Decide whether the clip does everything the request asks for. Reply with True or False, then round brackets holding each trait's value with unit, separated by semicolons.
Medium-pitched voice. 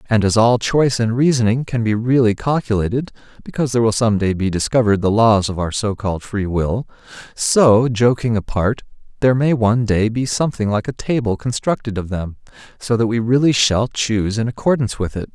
False (115 Hz)